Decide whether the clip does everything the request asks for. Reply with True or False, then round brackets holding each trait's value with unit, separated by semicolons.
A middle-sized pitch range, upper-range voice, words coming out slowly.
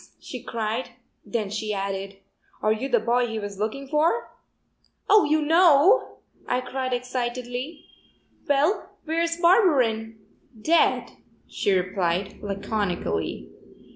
False (5.9 semitones; 245 Hz; 110 wpm)